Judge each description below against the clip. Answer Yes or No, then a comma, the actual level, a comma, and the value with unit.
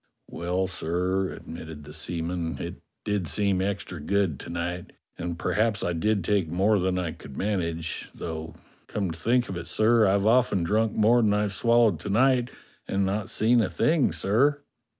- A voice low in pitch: Yes, very low, 95 Hz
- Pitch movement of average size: Yes, average, 4.1 semitones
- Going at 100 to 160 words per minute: No, average, 175 wpm